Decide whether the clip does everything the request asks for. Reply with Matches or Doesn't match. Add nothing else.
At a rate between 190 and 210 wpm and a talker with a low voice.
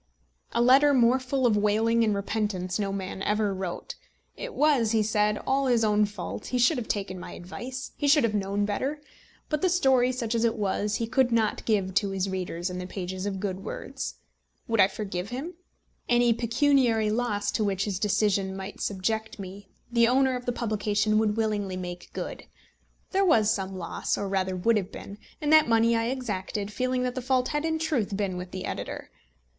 Doesn't match